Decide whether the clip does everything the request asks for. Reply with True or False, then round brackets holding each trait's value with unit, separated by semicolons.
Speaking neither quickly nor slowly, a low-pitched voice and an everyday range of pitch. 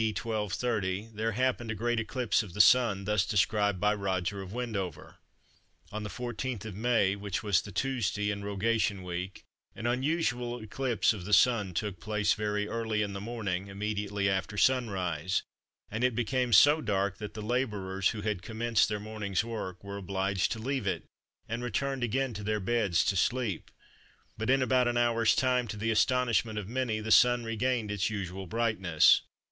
True (175 wpm; 105 Hz; 3.2 semitones)